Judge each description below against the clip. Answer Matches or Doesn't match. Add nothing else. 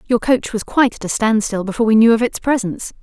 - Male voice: Doesn't match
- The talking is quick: Matches